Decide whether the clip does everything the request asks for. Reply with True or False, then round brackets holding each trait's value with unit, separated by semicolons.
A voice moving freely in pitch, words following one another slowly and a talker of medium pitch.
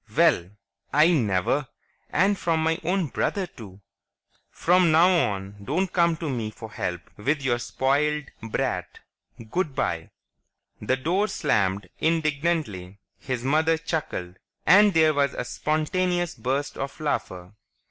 True (7.1 semitones; 130 wpm; 150 Hz)